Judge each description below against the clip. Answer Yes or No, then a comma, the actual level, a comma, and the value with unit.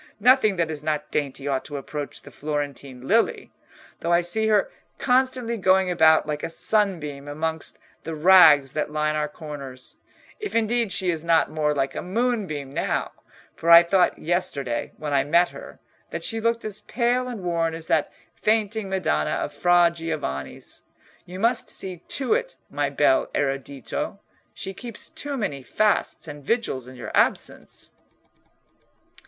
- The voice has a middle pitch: Yes, medium, 170 Hz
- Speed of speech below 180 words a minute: Yes, average, 160 wpm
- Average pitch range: No, wide, 6.4 semitones